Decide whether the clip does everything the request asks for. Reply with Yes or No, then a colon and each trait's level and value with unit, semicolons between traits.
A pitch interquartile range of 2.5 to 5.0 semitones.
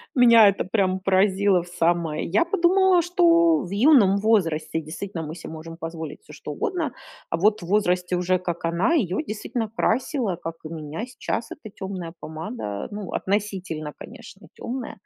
No: wide, 5.6 semitones